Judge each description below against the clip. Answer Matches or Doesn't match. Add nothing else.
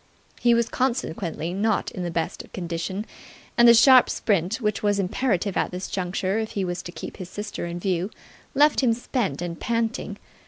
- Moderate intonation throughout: Matches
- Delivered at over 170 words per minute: Matches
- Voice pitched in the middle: Doesn't match